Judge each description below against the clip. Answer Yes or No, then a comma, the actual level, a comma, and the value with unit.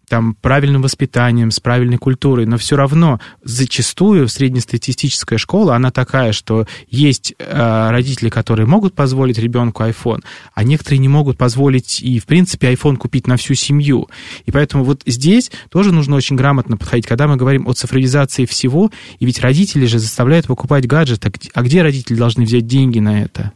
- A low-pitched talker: Yes, low, 130 Hz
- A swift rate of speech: Yes, fast, 170 wpm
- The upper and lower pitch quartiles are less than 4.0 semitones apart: Yes, average, 3.0 semitones